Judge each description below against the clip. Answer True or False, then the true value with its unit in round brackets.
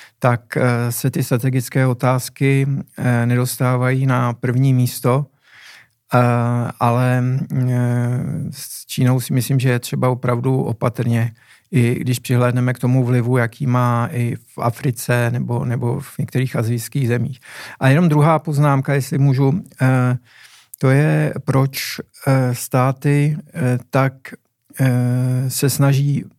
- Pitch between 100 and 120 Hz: False (130 Hz)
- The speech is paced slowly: True (110 wpm)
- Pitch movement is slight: True (1.9 semitones)